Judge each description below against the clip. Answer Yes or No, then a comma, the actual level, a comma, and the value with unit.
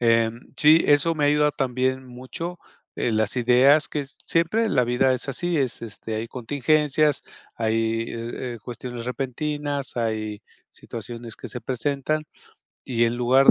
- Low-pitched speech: Yes, low, 125 Hz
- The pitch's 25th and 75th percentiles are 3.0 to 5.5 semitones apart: Yes, average, 3.8 semitones